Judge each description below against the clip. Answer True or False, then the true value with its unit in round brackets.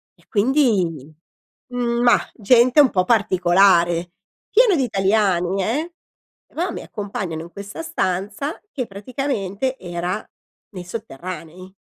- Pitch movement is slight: False (5.6 semitones)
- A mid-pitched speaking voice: False (200 Hz)